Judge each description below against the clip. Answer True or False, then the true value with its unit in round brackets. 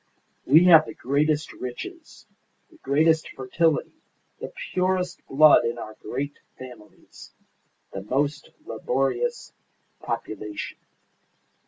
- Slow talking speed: True (100 wpm)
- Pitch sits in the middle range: True (145 Hz)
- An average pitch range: True (4.5 semitones)